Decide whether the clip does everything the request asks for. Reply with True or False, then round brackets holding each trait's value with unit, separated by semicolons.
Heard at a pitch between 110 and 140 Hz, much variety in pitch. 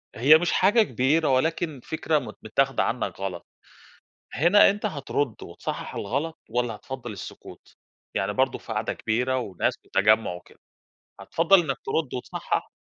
True (135 Hz; 5.9 semitones)